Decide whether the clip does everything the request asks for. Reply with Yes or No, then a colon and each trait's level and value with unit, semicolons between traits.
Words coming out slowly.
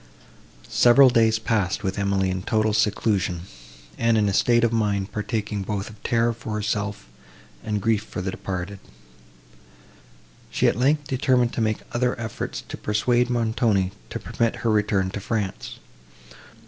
No: average, 150 wpm